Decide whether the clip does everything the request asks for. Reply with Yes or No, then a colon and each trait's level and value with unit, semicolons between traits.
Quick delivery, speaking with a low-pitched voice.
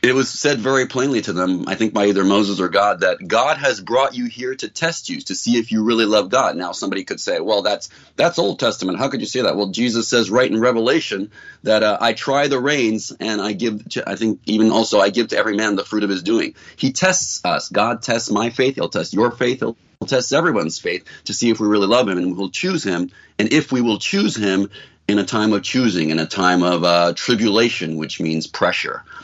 Yes: fast, 250 wpm; low, 110 Hz